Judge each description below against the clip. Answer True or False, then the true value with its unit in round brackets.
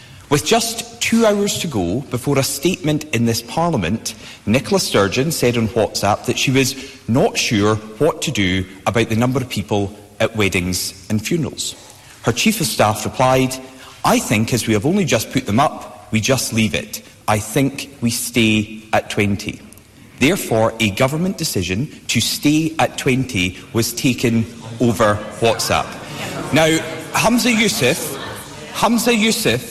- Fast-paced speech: False (155 wpm)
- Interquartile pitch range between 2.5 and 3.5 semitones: False (5.6 semitones)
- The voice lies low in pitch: True (120 Hz)